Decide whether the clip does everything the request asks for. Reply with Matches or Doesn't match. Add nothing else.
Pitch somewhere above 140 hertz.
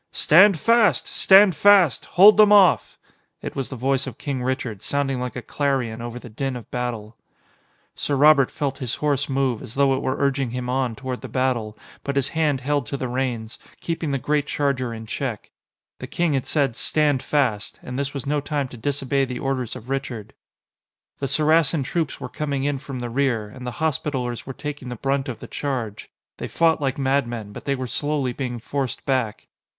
Doesn't match